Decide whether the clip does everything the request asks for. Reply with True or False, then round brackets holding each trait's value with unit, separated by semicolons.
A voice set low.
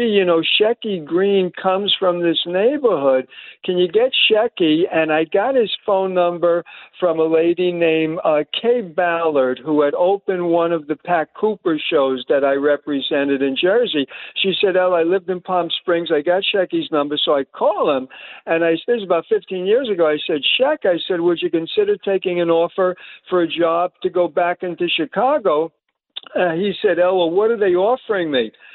False (180 Hz)